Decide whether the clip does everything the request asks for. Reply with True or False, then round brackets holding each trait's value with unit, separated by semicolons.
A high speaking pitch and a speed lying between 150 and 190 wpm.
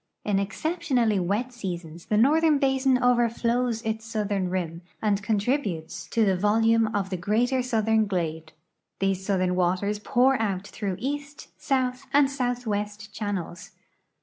False (215 Hz; 135 wpm)